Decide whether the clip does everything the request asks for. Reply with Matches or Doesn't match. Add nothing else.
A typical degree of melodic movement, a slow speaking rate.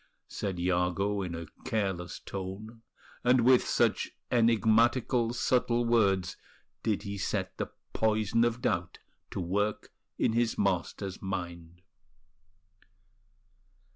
Matches